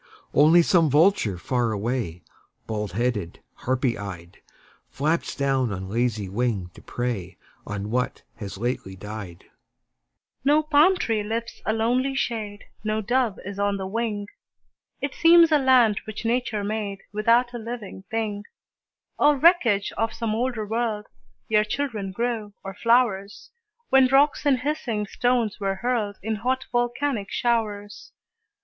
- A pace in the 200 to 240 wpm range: No, average, 140 wpm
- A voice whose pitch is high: Yes, high, 210 Hz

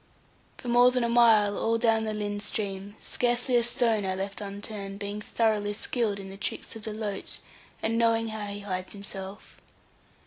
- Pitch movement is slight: Yes, narrow, 2.1 semitones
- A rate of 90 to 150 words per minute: No, average, 180 wpm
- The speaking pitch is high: Yes, high, 210 Hz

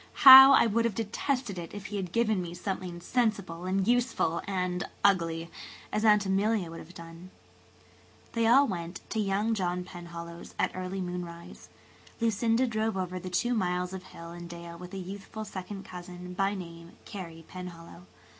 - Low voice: No, medium, 185 Hz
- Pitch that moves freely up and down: No, average, 3.6 semitones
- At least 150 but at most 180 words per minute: Yes, average, 165 wpm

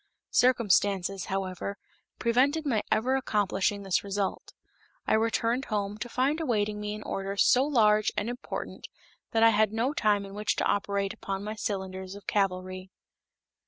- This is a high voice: Yes, high, 210 Hz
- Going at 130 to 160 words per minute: Yes, average, 155 wpm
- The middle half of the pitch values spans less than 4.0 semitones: Yes, average, 2.8 semitones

